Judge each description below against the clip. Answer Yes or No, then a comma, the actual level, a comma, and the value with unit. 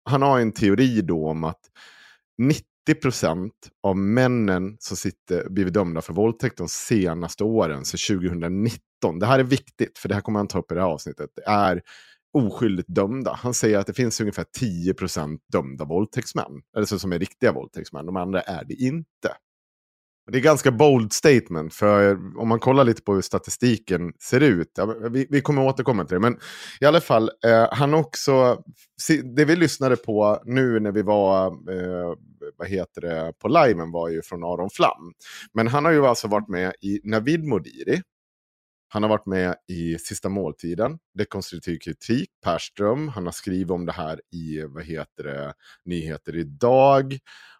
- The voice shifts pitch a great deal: Yes, wide, 5.9 semitones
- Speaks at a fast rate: No, average, 175 wpm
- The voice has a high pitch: No, low, 105 Hz